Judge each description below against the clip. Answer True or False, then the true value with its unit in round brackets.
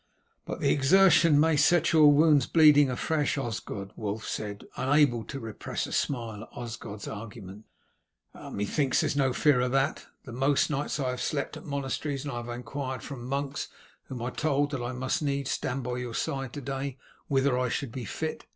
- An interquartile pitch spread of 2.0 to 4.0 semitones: True (3.1 semitones)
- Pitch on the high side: False (135 Hz)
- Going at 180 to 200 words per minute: True (190 wpm)